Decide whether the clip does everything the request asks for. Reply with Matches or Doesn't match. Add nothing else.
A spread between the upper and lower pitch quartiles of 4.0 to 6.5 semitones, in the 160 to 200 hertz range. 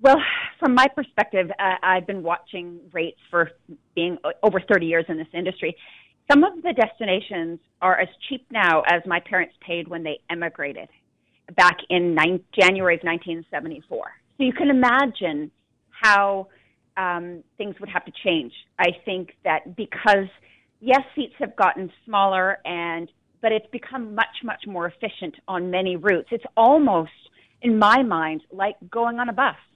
Matches